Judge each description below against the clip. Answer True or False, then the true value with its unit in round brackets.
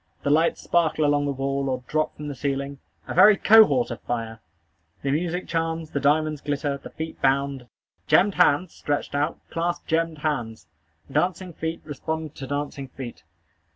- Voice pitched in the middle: True (145 Hz)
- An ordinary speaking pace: True (165 wpm)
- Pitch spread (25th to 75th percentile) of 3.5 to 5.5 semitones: False (2.9 semitones)